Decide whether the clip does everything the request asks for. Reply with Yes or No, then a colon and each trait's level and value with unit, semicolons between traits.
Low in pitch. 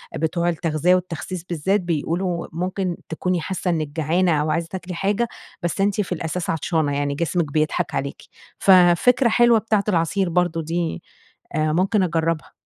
No: medium, 175 Hz